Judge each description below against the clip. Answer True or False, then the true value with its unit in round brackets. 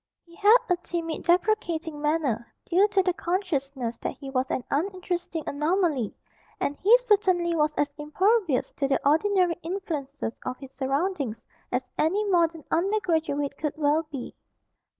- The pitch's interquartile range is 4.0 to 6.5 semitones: True (4.6 semitones)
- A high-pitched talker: True (325 Hz)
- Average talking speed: True (150 wpm)